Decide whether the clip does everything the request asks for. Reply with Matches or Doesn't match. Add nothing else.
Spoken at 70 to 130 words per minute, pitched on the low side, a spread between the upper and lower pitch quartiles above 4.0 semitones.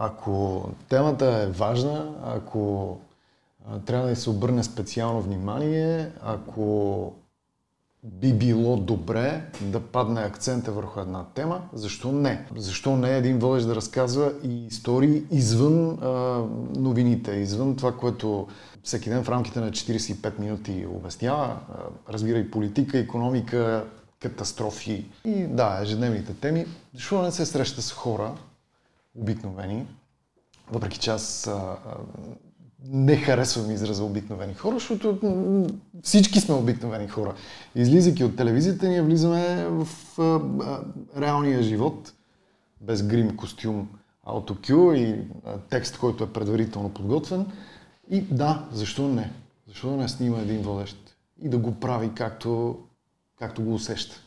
Matches